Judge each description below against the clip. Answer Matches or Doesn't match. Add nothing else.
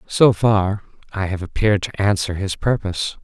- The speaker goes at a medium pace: Matches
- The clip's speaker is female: Doesn't match